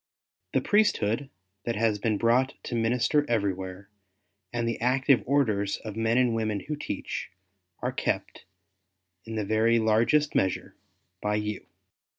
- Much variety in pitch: No, average, 2.9 semitones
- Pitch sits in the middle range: No, low, 115 Hz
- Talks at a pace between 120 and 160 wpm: Yes, average, 140 wpm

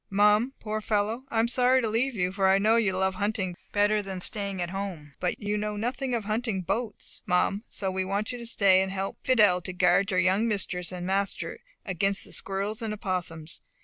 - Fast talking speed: Yes, fast, 215 wpm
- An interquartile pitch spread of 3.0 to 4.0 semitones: No, narrow, 2.6 semitones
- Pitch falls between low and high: No, high, 200 Hz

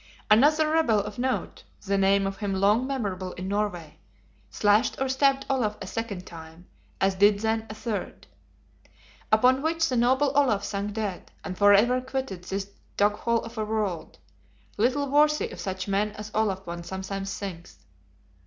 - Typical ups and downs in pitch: Yes, average, 4.5 semitones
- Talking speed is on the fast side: No, average, 160 wpm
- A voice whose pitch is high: Yes, high, 210 Hz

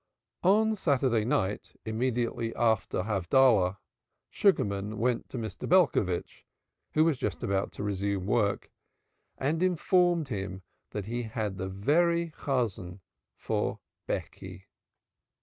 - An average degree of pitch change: No, wide, 6.6 semitones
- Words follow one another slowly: Yes, slow, 110 wpm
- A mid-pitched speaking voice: No, low, 115 Hz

